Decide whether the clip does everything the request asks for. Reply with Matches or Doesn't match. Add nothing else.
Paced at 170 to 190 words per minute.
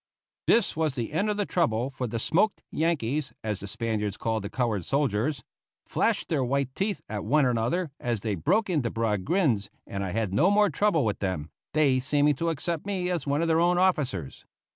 Doesn't match